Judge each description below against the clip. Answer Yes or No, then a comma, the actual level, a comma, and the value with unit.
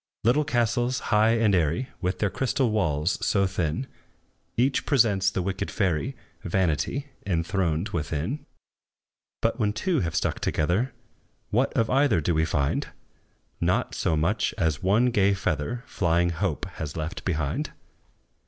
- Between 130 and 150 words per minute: Yes, average, 140 wpm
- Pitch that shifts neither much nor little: No, wide, 6.2 semitones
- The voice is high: No, very low, 95 Hz